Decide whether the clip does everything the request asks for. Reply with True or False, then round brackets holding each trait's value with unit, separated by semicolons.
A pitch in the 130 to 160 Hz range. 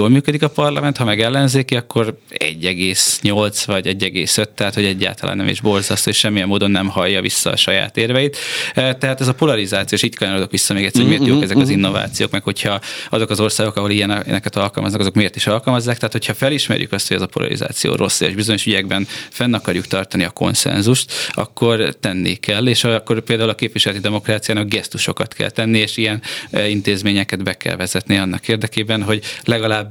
False (105 Hz)